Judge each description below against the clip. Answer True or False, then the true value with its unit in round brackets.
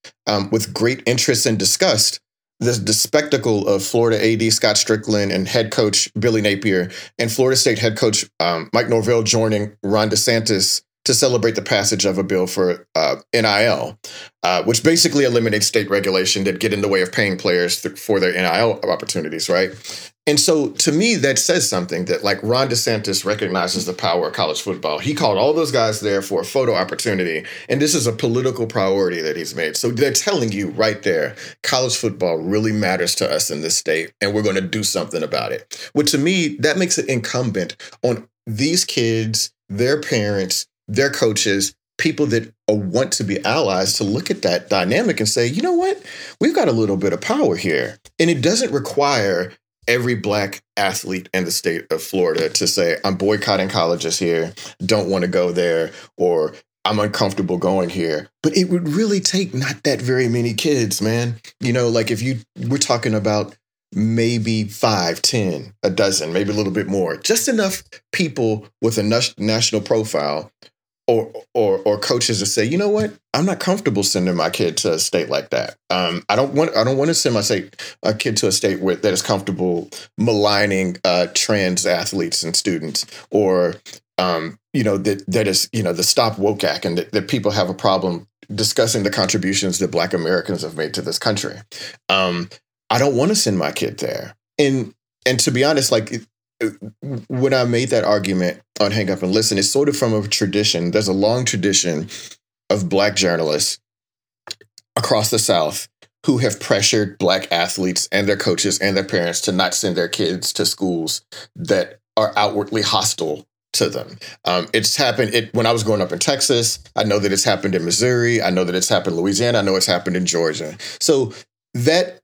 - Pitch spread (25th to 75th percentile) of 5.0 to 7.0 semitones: False (3.8 semitones)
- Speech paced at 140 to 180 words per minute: False (195 wpm)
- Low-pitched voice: True (110 Hz)